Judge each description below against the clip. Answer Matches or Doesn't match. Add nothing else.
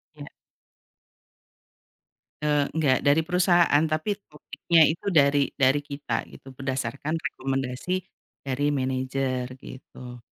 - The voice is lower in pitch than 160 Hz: Matches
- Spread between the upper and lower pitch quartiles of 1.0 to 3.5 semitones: Matches